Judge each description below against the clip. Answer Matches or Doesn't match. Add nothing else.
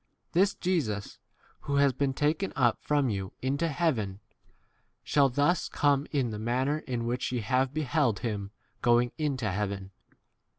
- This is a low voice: Matches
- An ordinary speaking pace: Matches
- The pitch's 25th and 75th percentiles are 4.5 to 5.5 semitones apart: Matches